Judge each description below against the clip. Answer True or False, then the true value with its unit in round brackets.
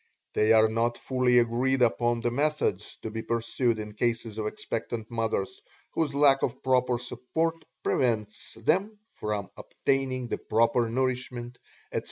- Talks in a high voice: False (120 Hz)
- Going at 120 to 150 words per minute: True (145 wpm)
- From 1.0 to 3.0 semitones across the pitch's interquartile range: True (2.4 semitones)